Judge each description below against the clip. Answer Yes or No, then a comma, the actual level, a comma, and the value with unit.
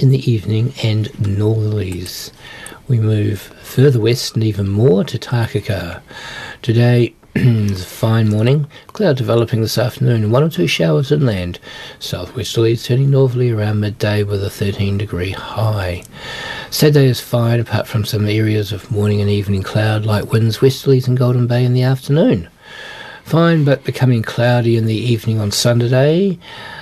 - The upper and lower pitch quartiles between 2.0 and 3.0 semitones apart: No, average, 3.7 semitones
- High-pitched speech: No, low, 115 Hz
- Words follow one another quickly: No, average, 155 wpm